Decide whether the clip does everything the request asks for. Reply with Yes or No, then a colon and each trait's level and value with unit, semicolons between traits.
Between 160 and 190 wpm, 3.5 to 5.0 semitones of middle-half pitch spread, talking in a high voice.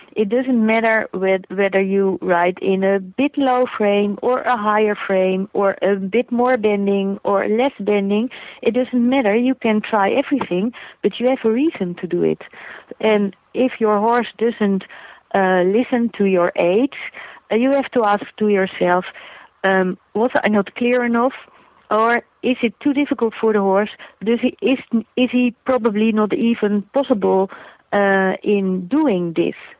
Yes: average, 165 wpm; average, 4.1 semitones; high, 215 Hz